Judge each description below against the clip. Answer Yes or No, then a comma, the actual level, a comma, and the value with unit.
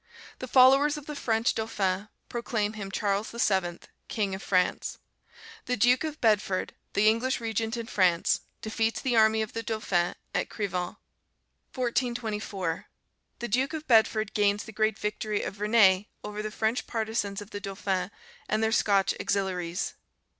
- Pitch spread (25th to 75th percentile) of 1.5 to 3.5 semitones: Yes, narrow, 2.6 semitones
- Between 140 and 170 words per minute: Yes, average, 155 wpm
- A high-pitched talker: Yes, high, 215 Hz